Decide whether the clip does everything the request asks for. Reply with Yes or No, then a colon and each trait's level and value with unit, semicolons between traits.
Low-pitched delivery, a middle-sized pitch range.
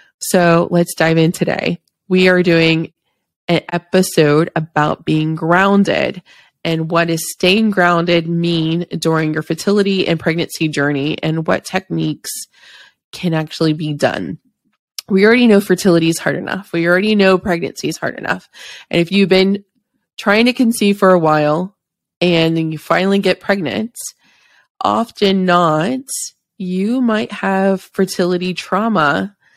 No: medium, 175 Hz; average, 3.2 semitones